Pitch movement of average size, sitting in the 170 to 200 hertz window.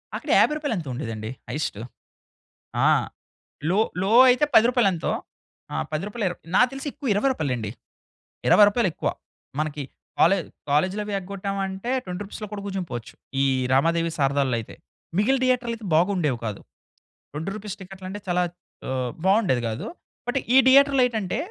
No: wide, 6.4 semitones; high, 190 Hz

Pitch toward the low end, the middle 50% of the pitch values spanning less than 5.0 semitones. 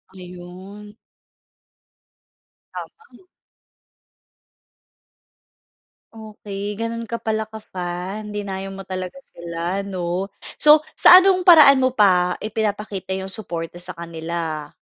No: high, 195 Hz; average, 3.5 semitones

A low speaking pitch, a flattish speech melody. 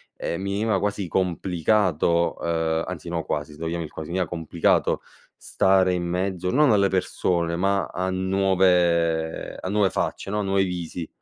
Yes: very low, 90 Hz; narrow, 2.3 semitones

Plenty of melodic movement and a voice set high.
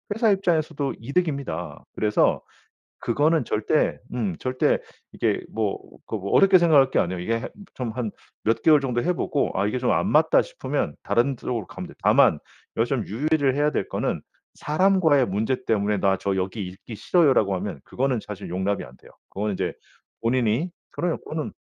No: wide, 6.5 semitones; low, 120 Hz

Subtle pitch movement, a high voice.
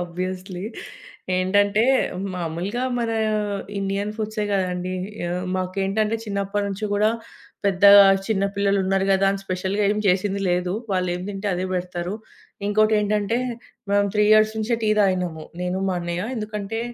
Yes: narrow, 2.3 semitones; high, 195 Hz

